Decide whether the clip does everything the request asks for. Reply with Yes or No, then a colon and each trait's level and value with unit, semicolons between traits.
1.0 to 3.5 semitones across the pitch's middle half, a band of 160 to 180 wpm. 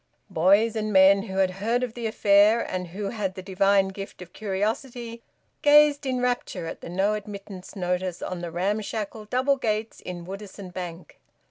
Yes: average, 3.2 semitones; average, 170 wpm